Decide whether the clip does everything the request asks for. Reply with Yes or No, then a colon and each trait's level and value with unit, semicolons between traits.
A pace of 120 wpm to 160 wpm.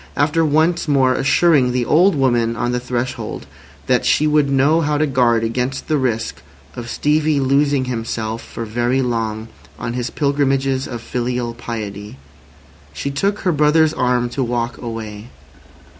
Yes: average, 155 wpm